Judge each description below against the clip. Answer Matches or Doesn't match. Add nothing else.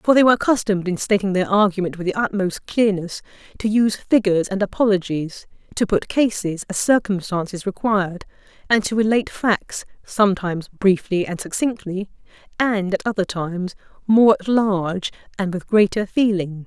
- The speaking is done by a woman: Matches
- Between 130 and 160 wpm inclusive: Matches